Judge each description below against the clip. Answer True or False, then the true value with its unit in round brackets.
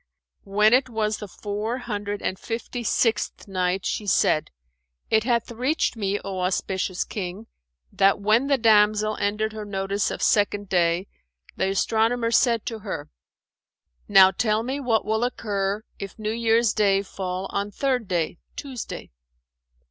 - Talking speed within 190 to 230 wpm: False (150 wpm)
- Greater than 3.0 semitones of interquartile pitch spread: False (2.7 semitones)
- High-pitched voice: True (210 Hz)